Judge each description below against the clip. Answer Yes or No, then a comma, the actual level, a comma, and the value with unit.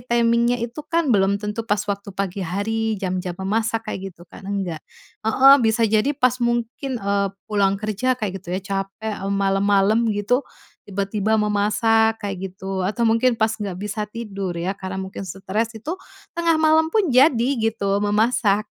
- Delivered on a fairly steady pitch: No, average, 3.0 semitones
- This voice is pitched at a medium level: No, high, 210 Hz